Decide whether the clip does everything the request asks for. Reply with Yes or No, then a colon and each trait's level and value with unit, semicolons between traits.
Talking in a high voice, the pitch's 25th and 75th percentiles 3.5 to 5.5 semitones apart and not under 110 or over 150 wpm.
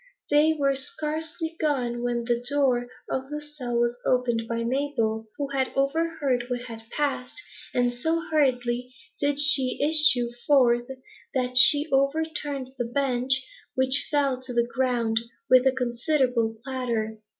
No: very high, 260 Hz; average, 3.1 semitones; average, 145 wpm